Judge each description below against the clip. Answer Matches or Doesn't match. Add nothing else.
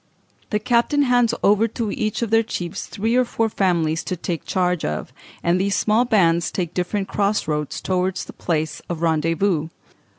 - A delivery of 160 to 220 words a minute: Matches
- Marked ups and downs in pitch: Doesn't match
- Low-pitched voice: Doesn't match